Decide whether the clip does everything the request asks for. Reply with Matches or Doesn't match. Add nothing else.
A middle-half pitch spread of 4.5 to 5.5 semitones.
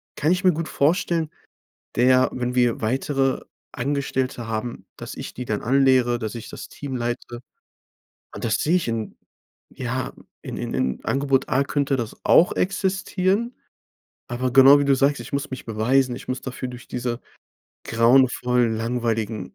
Doesn't match